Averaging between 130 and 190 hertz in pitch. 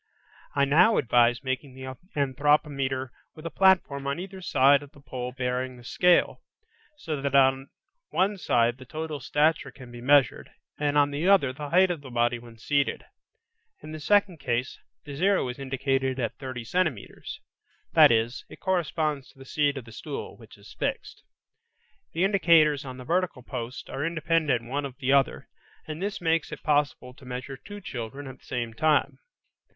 Yes: medium, 140 Hz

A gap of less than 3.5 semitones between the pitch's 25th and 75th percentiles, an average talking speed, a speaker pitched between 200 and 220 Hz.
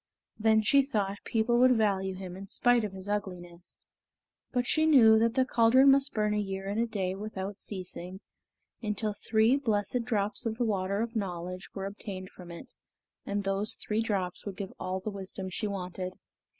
Yes: average, 2.9 semitones; average, 185 wpm; high, 205 Hz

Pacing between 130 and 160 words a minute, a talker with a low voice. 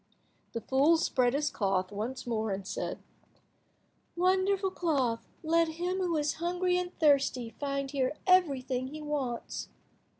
No: slow, 135 wpm; very high, 285 Hz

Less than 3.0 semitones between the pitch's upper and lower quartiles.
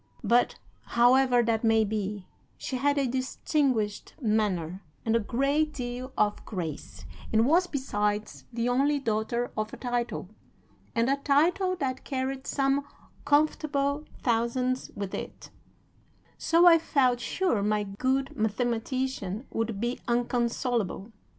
No: average, 3.9 semitones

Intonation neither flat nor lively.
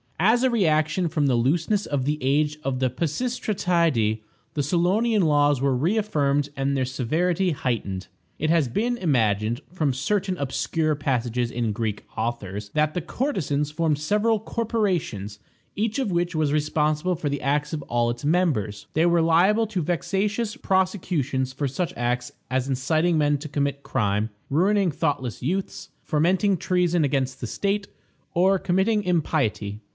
No: wide, 5.7 semitones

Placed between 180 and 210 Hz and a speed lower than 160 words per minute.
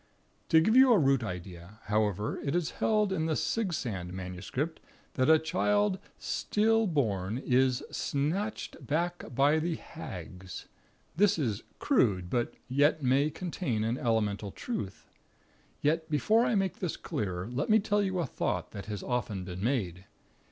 No: medium, 140 Hz; average, 150 wpm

